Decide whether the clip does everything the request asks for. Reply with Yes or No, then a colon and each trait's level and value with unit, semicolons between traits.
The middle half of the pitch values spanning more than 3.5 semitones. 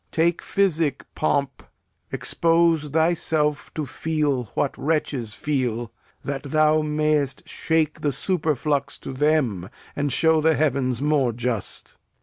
No: average, 2.9 semitones